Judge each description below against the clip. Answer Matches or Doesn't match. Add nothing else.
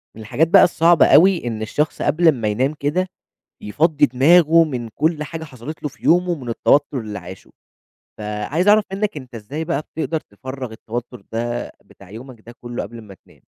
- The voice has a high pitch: Doesn't match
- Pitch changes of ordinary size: Doesn't match